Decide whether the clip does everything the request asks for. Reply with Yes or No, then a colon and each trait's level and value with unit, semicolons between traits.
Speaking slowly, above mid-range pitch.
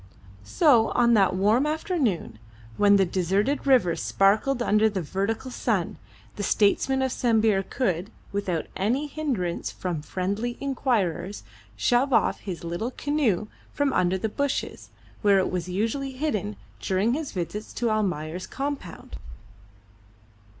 Yes: slow, 130 wpm; high, 215 Hz